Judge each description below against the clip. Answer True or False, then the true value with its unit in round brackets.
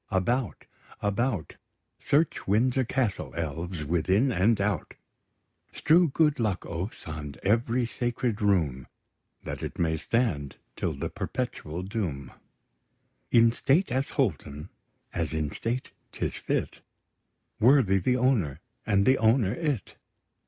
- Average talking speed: False (120 wpm)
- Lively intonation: True (6.8 semitones)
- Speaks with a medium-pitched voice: False (105 Hz)